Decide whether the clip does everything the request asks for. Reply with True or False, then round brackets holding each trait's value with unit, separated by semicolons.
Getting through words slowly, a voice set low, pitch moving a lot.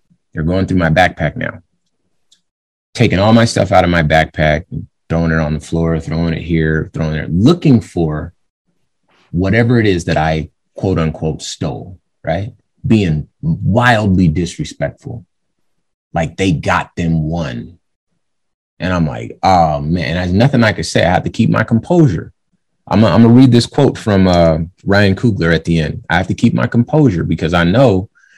False (175 wpm; 90 Hz; 5.8 semitones)